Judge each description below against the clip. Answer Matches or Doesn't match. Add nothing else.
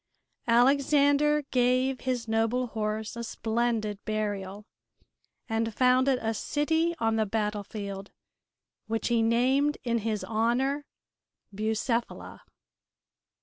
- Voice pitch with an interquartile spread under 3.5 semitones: Matches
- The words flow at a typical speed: Doesn't match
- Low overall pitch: Doesn't match